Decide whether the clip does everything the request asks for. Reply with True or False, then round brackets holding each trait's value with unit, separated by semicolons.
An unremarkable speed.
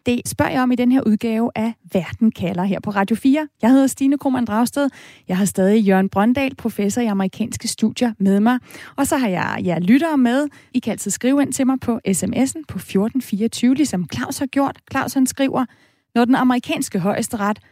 True (205 wpm)